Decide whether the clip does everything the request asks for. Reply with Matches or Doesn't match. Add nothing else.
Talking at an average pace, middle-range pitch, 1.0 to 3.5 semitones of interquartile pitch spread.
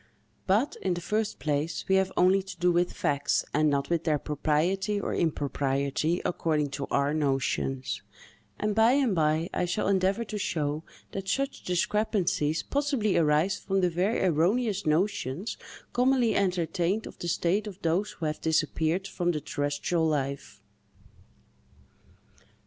Doesn't match